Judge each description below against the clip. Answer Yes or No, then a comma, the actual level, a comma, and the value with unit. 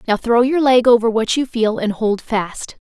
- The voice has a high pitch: Yes, high, 230 Hz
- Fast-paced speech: Yes, fast, 230 wpm